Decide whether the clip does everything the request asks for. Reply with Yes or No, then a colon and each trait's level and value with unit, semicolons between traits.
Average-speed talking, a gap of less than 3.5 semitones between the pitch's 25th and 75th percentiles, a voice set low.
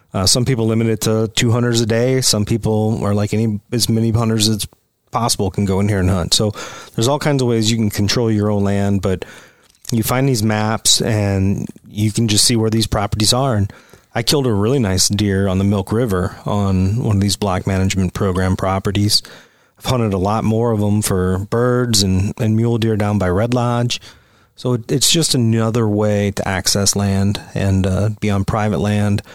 No: fast, 210 wpm; narrow, 2.5 semitones; low, 105 Hz